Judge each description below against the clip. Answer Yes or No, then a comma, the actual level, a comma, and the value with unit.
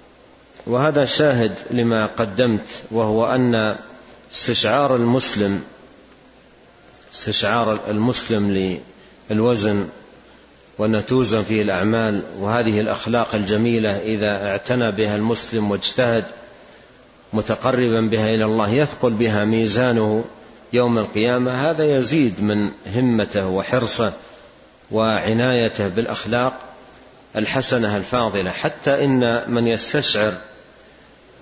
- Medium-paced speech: Yes, average, 85 wpm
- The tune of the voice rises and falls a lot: No, average, 2.7 semitones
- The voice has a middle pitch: No, low, 115 Hz